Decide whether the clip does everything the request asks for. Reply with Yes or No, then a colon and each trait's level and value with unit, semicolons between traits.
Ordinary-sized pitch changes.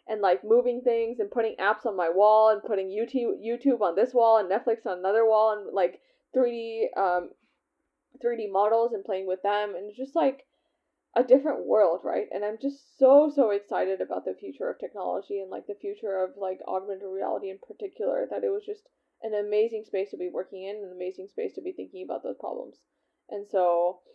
No: wide, 7.7 semitones